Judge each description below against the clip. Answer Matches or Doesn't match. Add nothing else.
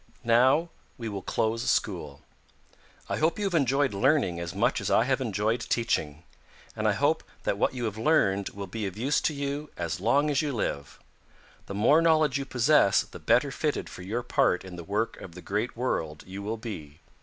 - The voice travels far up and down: Matches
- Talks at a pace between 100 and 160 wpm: Doesn't match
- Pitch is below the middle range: Matches